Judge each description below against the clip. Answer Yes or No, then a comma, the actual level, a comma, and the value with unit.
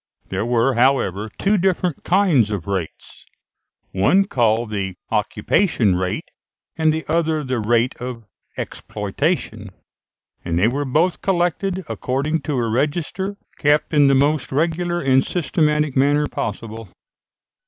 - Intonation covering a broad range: Yes, wide, 6.3 semitones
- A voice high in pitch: No, medium, 140 Hz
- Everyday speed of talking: No, slow, 130 wpm